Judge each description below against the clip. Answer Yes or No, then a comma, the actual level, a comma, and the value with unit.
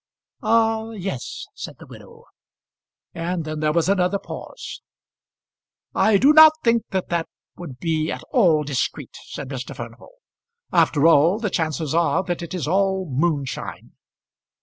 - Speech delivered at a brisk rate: No, average, 145 wpm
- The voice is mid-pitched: Yes, medium, 170 Hz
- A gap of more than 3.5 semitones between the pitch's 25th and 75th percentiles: Yes, average, 4.3 semitones